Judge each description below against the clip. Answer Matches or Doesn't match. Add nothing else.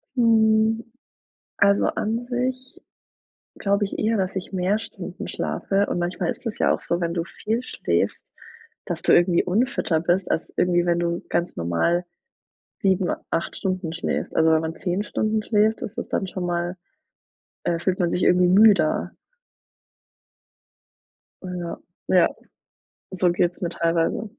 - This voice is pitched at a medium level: Matches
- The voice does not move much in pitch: Doesn't match